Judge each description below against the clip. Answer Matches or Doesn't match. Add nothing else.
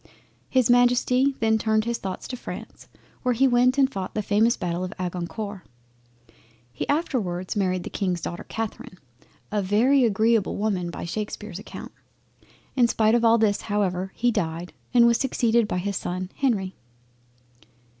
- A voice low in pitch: Doesn't match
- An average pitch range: Matches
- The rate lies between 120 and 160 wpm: Matches